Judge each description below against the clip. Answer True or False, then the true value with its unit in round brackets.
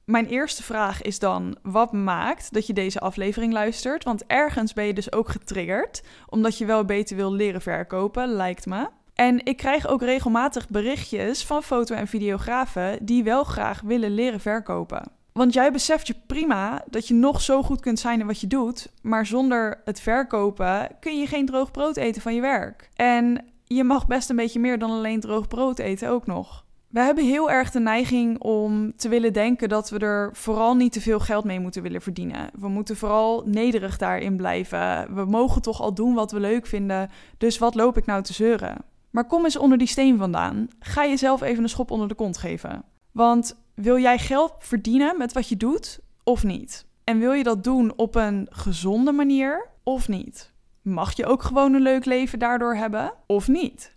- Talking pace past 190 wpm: True (200 wpm)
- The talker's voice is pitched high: True (230 Hz)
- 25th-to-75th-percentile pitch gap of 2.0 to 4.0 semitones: True (3.4 semitones)